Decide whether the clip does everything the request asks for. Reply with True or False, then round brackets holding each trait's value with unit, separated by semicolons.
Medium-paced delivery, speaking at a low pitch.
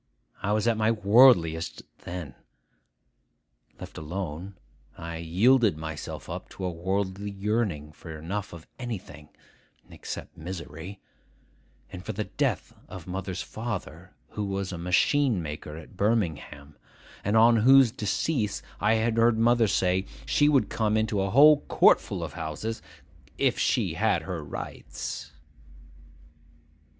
False (130 wpm; 100 Hz)